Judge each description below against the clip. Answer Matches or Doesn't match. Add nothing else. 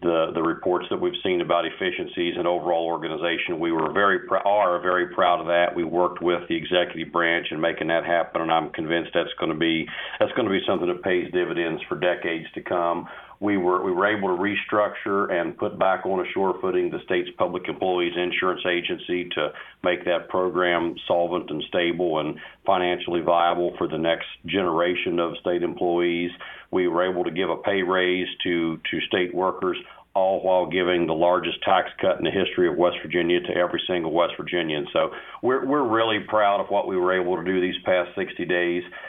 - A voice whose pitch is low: Matches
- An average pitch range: Doesn't match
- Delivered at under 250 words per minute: Matches